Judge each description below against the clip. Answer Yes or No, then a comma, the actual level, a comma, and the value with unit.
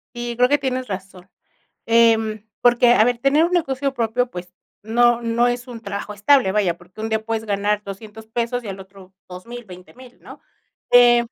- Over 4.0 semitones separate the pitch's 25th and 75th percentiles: No, average, 3.2 semitones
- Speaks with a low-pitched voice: No, high, 230 Hz